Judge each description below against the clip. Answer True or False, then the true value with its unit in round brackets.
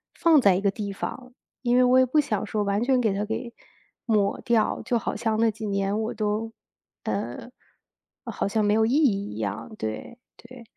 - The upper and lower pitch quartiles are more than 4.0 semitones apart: False (3.3 semitones)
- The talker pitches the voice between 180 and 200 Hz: False (220 Hz)